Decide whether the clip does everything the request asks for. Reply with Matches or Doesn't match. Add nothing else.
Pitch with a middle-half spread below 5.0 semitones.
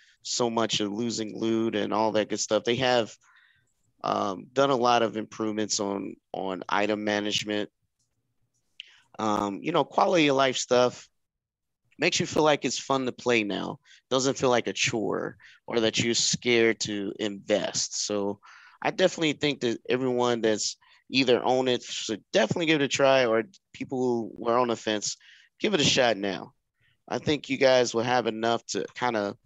Matches